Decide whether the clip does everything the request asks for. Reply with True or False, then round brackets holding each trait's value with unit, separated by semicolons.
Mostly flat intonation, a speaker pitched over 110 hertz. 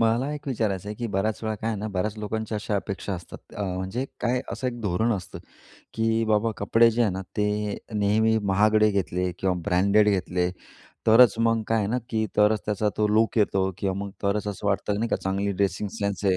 False (2.3 semitones; 105 Hz)